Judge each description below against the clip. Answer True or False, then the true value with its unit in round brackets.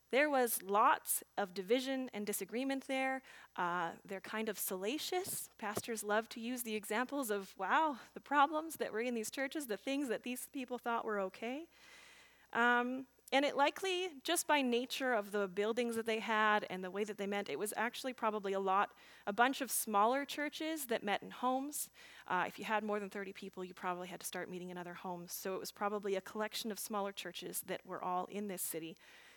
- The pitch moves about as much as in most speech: True (4.7 semitones)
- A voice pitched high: True (220 Hz)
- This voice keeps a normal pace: False (210 wpm)